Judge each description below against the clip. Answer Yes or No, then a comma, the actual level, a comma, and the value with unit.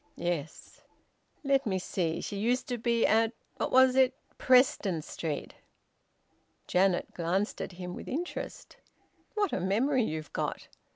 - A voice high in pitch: Yes, high, 215 Hz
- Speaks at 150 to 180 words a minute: No, slow, 135 wpm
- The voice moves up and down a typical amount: No, wide, 6.3 semitones